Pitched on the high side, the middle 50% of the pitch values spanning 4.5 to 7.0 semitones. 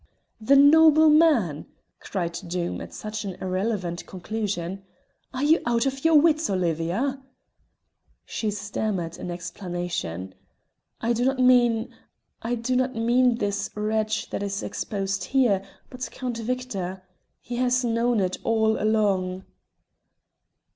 Yes: high, 220 Hz; average, 5.2 semitones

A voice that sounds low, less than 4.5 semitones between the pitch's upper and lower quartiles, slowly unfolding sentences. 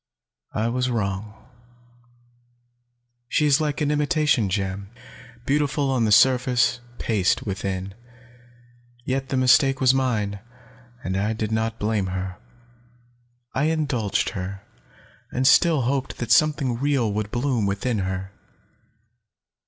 No: low, 120 Hz; average, 5.1 semitones; slow, 120 wpm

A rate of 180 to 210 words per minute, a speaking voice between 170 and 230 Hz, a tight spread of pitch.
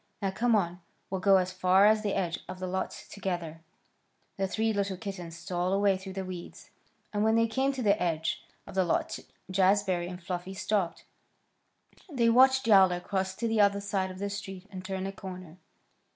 Yes: average, 195 wpm; high, 190 Hz; narrow, 1.9 semitones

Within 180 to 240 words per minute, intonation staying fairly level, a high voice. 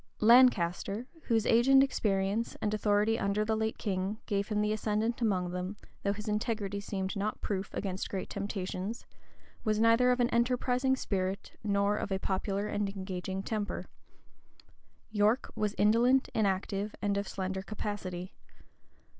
No: average, 145 wpm; narrow, 2.3 semitones; high, 210 Hz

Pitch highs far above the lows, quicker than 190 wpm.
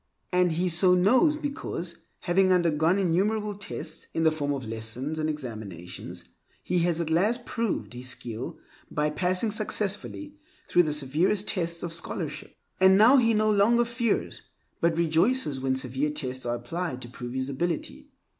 No: wide, 6.2 semitones; average, 160 wpm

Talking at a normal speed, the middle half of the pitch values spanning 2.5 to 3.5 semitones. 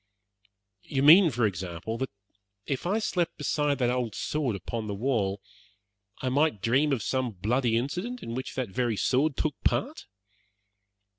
No: average, 155 wpm; average, 4.8 semitones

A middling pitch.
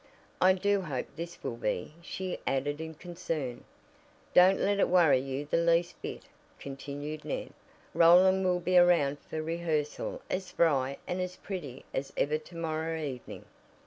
Yes: medium, 165 Hz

